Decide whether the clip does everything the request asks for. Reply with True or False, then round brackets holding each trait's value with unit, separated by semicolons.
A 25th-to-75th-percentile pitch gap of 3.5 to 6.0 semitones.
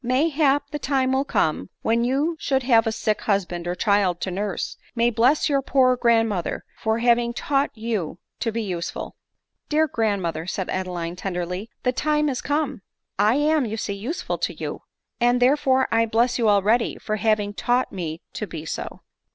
True (4.9 semitones)